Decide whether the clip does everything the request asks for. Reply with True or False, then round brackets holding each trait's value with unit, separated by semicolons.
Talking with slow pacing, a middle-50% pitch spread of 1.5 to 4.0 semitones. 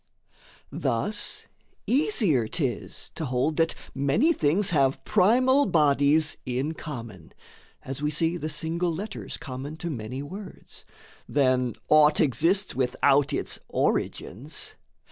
False (115 wpm; 4.7 semitones)